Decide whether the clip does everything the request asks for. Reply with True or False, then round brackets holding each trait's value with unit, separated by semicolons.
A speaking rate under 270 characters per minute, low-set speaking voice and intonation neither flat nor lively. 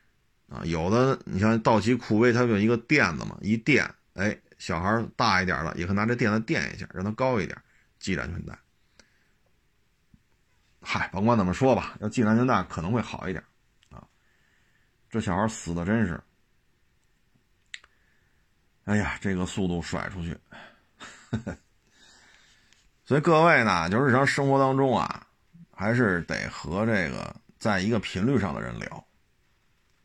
True (215 characters per minute; 110 Hz; 3.8 semitones)